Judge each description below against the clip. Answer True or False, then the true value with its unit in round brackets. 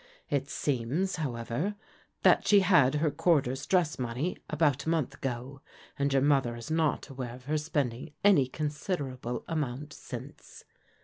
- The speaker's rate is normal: True (145 wpm)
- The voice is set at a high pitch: False (145 Hz)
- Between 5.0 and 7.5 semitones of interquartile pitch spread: False (3.8 semitones)